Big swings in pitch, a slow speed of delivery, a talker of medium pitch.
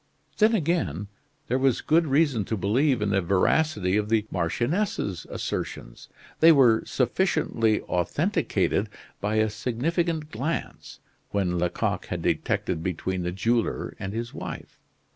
No: wide, 7.6 semitones; slow, 130 wpm; low, 110 Hz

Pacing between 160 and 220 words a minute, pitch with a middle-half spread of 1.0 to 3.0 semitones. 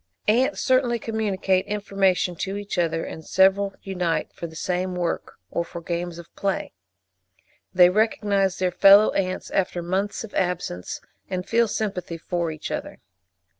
No: average, 150 wpm; narrow, 2.5 semitones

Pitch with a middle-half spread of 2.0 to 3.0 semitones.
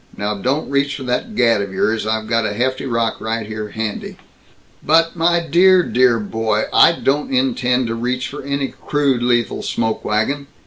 No: average, 4.0 semitones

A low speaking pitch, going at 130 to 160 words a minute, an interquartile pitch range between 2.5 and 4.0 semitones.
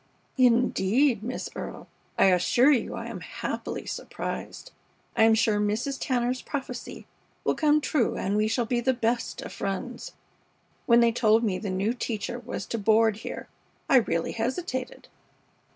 No: high, 235 Hz; average, 155 wpm; average, 2.8 semitones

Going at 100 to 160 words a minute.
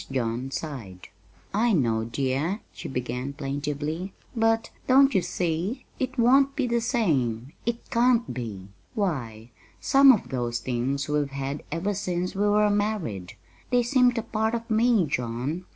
Yes: average, 150 wpm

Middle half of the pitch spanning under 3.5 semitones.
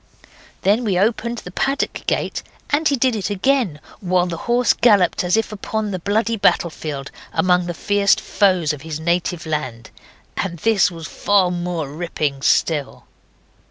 No: average, 4.9 semitones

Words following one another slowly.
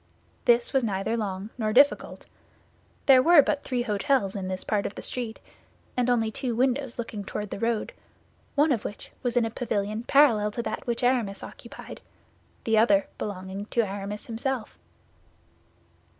No: average, 165 wpm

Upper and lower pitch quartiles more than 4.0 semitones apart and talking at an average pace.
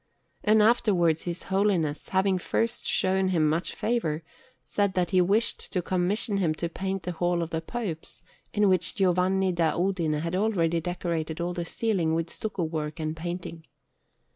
No: average, 2.8 semitones; average, 165 wpm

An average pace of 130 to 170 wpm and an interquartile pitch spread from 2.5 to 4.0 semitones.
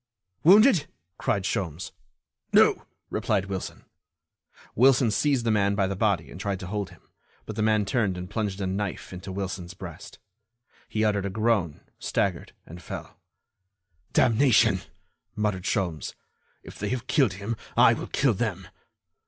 Yes: average, 150 wpm; average, 3.1 semitones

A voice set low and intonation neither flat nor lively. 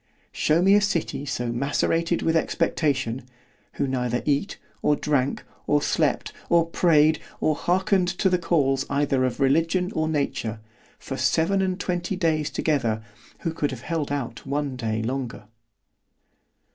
No: medium, 150 Hz; average, 4.2 semitones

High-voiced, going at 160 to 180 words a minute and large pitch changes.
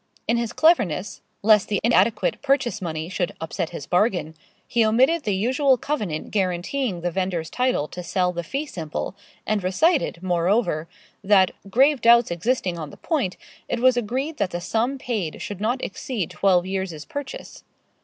Yes: high, 205 Hz; average, 165 wpm; wide, 6.0 semitones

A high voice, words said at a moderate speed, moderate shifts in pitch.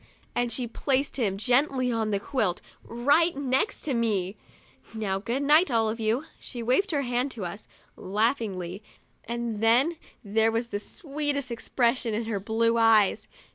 Yes: high, 235 Hz; average, 165 wpm; average, 3.5 semitones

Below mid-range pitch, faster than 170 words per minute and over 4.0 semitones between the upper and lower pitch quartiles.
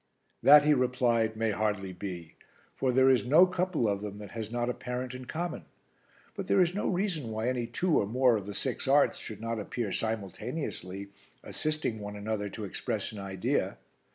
Yes: low, 115 Hz; average, 190 wpm; average, 4.4 semitones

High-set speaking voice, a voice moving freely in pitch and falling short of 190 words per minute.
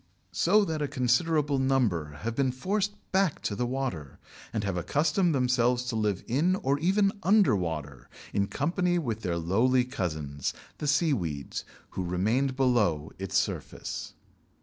No: low, 125 Hz; wide, 7.9 semitones; average, 150 wpm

